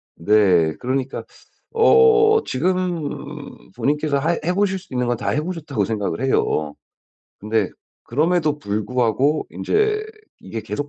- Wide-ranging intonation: Yes, wide, 8.3 semitones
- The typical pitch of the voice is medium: Yes, medium, 145 Hz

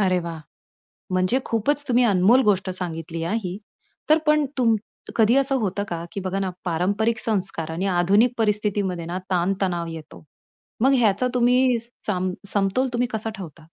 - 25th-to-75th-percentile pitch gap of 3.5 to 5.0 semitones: Yes, average, 4.7 semitones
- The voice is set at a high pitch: Yes, high, 200 Hz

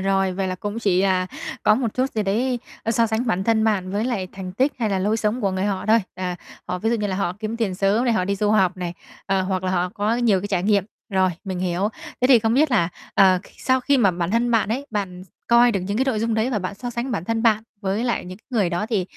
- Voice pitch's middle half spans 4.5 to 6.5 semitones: No, average, 3.5 semitones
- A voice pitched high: Yes, high, 205 Hz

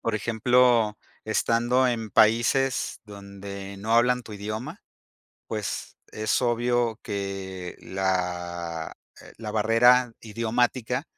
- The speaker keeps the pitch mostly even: No, average, 3.3 semitones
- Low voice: Yes, low, 110 Hz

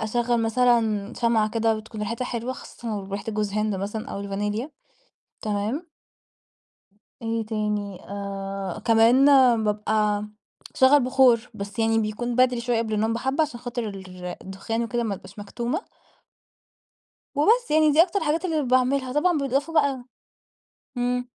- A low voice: No, high, 230 Hz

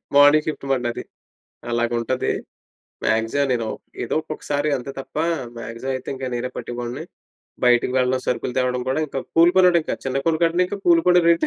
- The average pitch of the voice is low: Yes, low, 130 Hz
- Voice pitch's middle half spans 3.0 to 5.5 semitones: Yes, average, 4.3 semitones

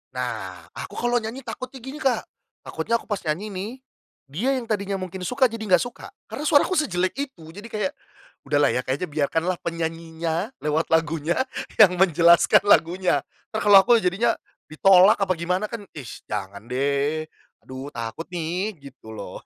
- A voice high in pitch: No, medium, 180 Hz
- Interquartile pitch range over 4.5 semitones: Yes, average, 5.2 semitones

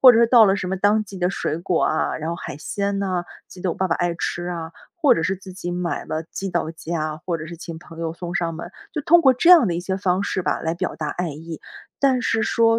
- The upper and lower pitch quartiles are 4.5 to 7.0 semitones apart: No, average, 3.2 semitones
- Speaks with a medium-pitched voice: Yes, medium, 180 Hz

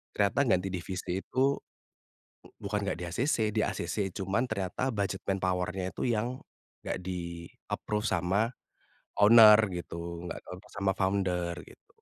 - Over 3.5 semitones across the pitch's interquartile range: No, average, 2.9 semitones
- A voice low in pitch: Yes, very low, 95 Hz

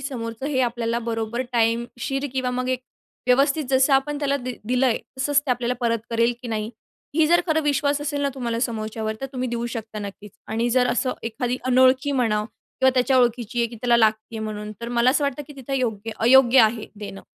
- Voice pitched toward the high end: Yes, high, 245 Hz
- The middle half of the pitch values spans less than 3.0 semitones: Yes, narrow, 2.6 semitones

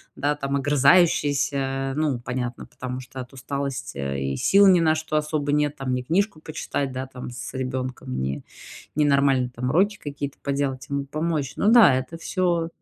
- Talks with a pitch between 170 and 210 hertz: No, medium, 140 Hz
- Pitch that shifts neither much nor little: Yes, average, 3.0 semitones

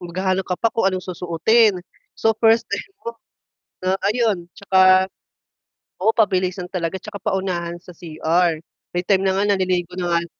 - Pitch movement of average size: No, narrow, 2.3 semitones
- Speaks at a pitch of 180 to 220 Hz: Yes, medium, 185 Hz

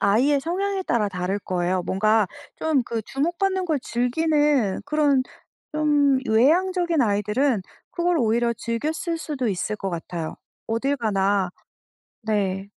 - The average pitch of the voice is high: Yes, high, 240 Hz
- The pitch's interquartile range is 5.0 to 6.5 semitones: No, wide, 7.1 semitones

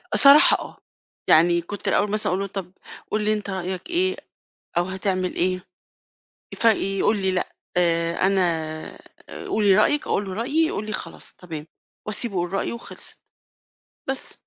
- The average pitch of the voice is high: Yes, high, 195 Hz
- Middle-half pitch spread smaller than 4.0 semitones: Yes, average, 3.1 semitones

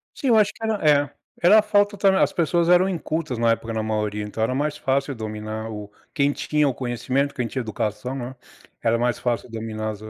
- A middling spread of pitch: No, wide, 7.0 semitones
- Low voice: Yes, low, 125 Hz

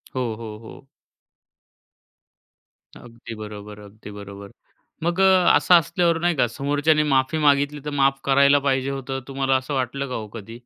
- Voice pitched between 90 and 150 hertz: Yes, low, 135 Hz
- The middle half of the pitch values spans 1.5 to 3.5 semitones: No, average, 3.9 semitones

